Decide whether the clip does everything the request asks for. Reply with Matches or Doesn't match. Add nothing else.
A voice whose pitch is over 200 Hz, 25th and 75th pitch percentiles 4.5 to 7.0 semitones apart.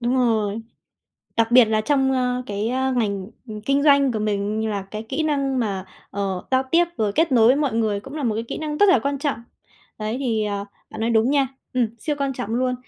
Doesn't match